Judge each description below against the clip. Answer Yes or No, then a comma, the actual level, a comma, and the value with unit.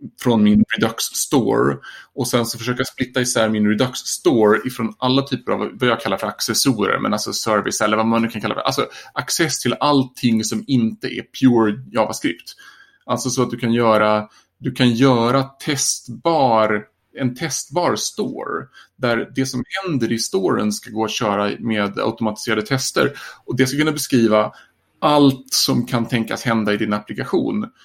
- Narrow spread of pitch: No, average, 3.2 semitones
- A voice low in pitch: Yes, low, 120 Hz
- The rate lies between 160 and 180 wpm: Yes, average, 170 wpm